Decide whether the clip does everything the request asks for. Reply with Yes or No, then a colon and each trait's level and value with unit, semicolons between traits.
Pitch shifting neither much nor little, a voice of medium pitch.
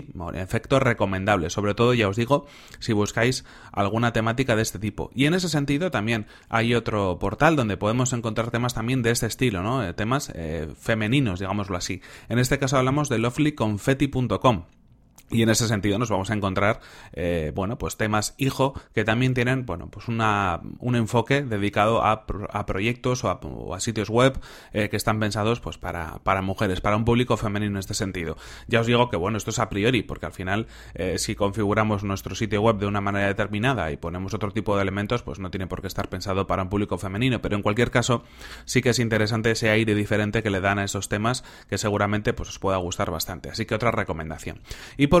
No: average, 3.2 semitones; low, 110 Hz